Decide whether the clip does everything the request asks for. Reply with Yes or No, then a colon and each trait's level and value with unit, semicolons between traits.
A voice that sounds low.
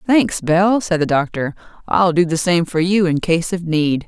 No: medium, 175 Hz